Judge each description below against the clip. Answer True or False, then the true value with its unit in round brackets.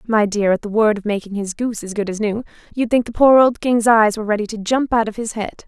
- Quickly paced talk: True (295 wpm)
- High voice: True (220 Hz)